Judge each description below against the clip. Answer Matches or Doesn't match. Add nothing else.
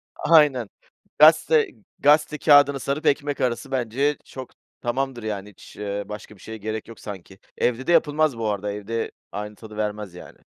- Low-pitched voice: Matches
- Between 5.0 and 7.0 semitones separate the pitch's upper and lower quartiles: Matches